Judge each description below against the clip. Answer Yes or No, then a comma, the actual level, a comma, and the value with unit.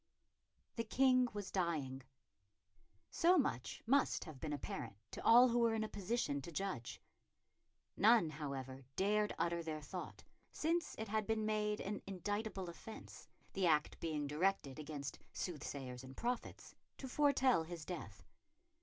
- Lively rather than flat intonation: Yes, wide, 6.8 semitones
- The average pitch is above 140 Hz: Yes, high, 190 Hz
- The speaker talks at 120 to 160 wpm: Yes, average, 145 wpm